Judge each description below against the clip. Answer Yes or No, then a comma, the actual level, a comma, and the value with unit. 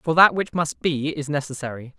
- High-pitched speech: No, medium, 150 Hz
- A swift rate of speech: Yes, fast, 210 wpm